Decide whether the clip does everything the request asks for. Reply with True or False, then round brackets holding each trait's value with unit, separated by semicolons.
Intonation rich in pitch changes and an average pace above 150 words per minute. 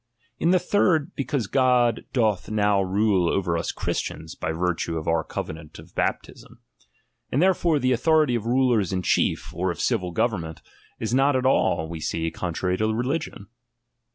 True (6.7 semitones; 170 wpm)